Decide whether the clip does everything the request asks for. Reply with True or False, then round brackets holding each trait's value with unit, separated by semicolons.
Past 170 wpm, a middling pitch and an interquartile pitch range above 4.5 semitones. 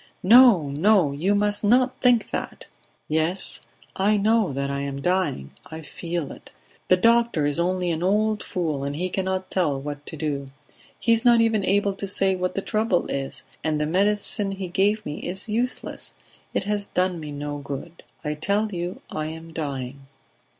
True (180 wpm; 180 Hz; 5.5 semitones)